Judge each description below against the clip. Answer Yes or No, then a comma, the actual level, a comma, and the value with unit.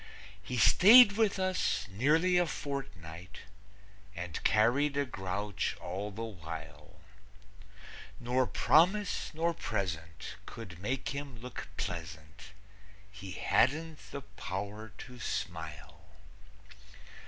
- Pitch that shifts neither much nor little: No, wide, 7.8 semitones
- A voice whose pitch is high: No, low, 110 Hz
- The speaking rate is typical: No, slow, 100 wpm